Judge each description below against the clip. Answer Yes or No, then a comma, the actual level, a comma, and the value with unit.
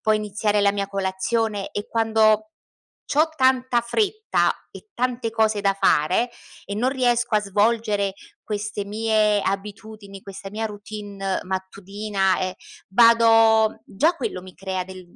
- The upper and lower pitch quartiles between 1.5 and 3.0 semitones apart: Yes, narrow, 2.5 semitones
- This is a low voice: No, high, 210 Hz